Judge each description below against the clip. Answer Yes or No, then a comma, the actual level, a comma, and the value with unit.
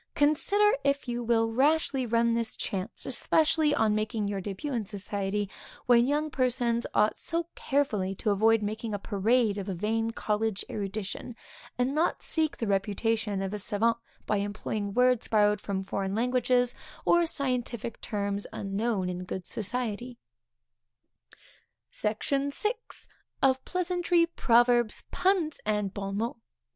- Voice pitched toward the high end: Yes, high, 225 Hz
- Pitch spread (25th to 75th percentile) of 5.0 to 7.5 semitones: No, average, 4.1 semitones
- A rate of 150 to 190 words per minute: No, average, 140 wpm